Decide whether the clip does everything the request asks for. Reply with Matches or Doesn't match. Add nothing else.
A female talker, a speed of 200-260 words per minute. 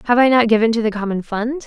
Doesn't match